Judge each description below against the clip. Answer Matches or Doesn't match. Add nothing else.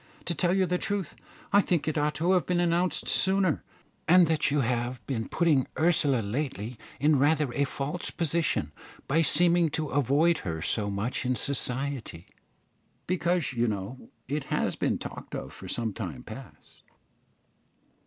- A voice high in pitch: Doesn't match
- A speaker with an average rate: Matches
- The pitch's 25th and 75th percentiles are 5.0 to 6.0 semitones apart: Matches